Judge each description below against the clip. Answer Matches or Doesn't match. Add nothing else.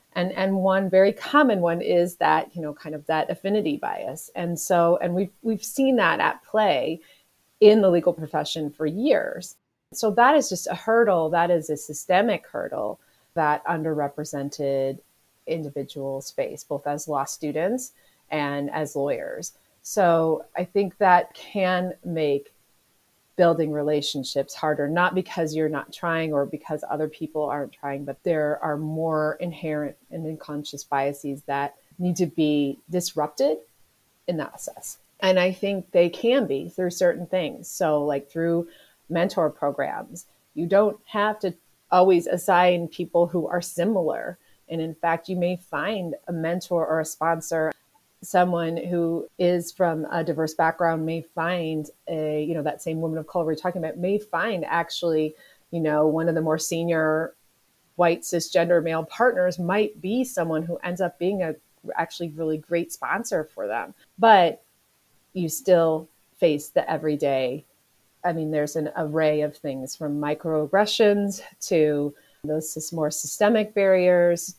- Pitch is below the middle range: Doesn't match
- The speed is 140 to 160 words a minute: Matches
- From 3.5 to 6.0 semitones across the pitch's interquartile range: Doesn't match